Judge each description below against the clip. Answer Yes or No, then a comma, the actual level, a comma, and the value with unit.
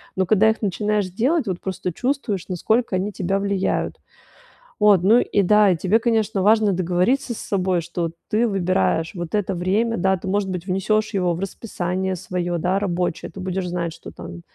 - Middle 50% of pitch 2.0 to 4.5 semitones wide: Yes, average, 2.9 semitones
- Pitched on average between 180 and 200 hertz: Yes, high, 190 Hz